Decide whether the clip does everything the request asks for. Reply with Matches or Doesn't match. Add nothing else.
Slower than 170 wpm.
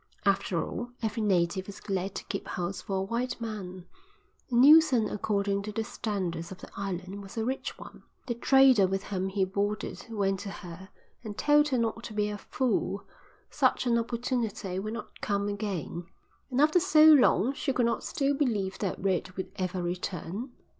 Doesn't match